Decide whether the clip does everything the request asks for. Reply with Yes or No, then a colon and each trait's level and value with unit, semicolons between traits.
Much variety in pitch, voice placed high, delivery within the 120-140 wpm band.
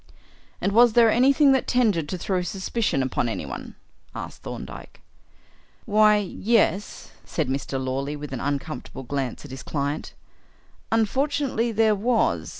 Yes: wide, 8.7 semitones; high, 195 Hz; slow, 135 wpm